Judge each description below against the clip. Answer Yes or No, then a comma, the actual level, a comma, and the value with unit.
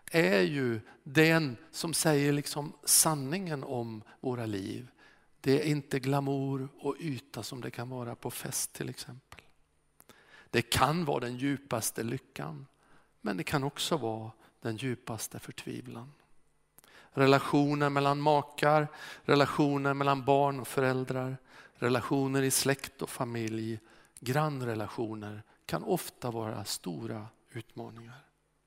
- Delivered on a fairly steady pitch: No, average, 3.6 semitones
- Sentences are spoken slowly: Yes, slow, 120 wpm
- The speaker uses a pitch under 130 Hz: No, low, 135 Hz